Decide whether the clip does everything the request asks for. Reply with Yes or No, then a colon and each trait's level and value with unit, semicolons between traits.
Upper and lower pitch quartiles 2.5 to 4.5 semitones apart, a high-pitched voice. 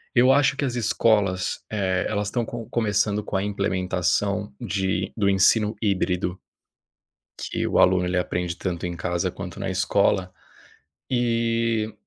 No: average, 3.4 semitones; low, 100 Hz